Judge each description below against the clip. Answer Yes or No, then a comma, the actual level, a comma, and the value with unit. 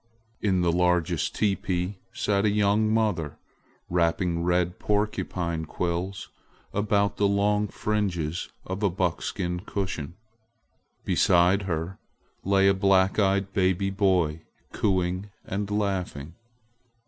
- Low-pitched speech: Yes, very low, 95 Hz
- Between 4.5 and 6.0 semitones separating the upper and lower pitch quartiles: No, narrow, 2.4 semitones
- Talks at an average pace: No, slow, 110 wpm